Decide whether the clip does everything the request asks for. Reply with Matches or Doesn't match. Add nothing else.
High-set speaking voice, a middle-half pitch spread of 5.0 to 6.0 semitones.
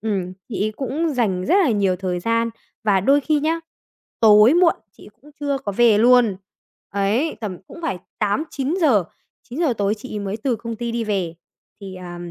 Matches